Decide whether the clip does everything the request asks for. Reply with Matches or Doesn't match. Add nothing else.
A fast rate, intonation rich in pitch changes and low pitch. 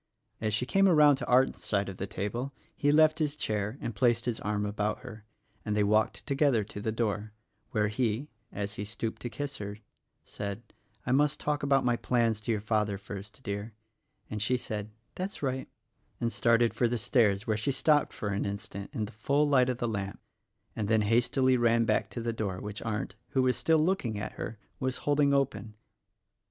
Doesn't match